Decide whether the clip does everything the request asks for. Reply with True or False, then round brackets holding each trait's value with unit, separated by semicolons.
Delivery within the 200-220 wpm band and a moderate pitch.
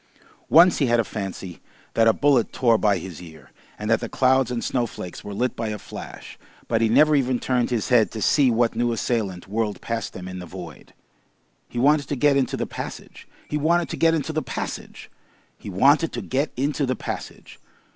False (205 wpm; 120 Hz)